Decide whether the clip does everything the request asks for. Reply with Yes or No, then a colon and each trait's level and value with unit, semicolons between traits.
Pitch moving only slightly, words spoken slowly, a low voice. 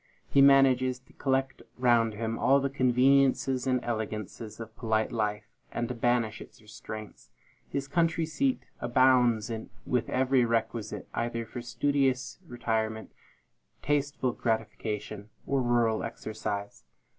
No: average, 3.1 semitones; slow, 120 wpm; low, 120 Hz